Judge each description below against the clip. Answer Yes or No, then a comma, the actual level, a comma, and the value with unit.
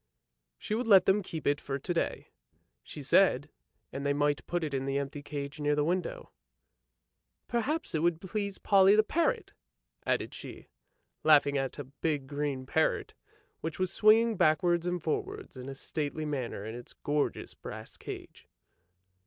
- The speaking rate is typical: Yes, average, 170 wpm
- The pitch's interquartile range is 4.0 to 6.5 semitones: Yes, average, 4.9 semitones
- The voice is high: No, medium, 150 Hz